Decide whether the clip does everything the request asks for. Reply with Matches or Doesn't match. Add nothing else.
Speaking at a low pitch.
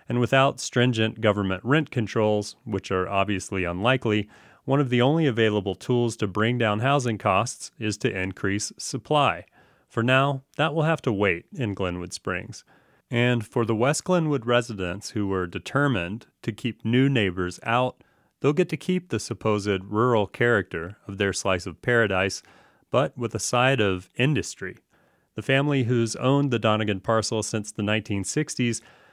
Matches